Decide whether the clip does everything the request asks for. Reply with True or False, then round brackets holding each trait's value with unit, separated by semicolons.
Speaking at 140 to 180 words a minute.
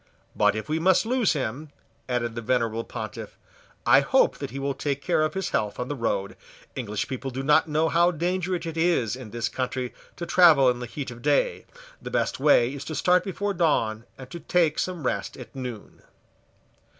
False (205 wpm)